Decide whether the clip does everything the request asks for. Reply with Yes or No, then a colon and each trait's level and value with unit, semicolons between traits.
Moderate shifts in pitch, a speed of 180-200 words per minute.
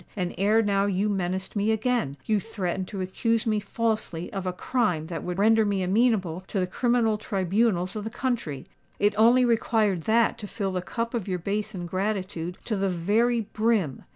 Yes: average, 3.4 semitones; average, 185 wpm